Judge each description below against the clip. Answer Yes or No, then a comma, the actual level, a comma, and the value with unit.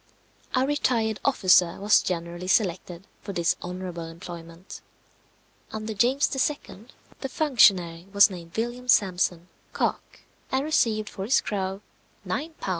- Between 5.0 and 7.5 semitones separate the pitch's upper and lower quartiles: Yes, average, 5.3 semitones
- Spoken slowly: Yes, slow, 125 wpm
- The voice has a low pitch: No, high, 195 Hz